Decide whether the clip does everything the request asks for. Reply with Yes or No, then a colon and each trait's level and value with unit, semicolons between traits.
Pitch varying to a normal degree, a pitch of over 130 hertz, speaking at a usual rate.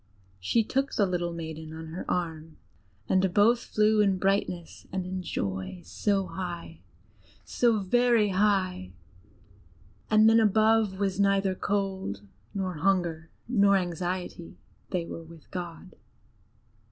No: average, 3.2 semitones; medium, 185 Hz; slow, 125 wpm